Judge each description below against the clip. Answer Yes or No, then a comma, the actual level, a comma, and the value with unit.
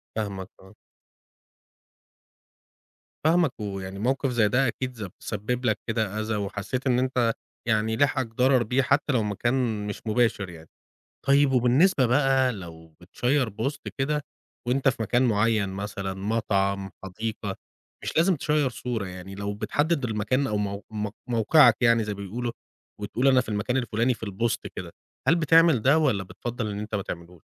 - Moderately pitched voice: No, low, 115 Hz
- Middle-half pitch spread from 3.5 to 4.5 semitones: Yes, average, 4.2 semitones